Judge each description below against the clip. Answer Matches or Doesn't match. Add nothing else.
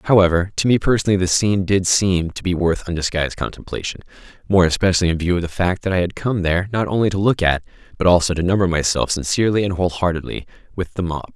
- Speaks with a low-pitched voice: Matches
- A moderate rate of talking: Doesn't match